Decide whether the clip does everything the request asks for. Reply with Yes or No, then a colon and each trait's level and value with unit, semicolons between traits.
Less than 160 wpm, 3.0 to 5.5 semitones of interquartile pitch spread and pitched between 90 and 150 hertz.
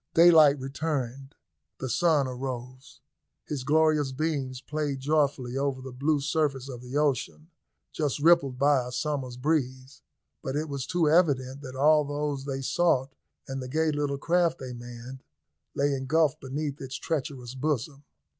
No: average, 150 wpm; narrow, 2.6 semitones; medium, 140 Hz